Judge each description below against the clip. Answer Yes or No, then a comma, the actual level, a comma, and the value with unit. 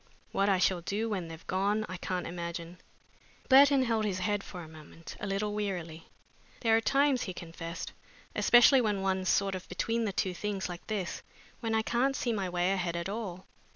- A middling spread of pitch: Yes, average, 3.8 semitones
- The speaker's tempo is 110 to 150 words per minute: No, average, 195 wpm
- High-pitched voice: Yes, high, 195 Hz